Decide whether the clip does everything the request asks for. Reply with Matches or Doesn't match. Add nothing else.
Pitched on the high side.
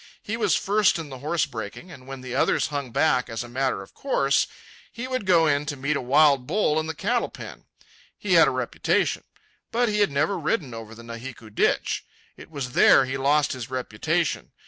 Doesn't match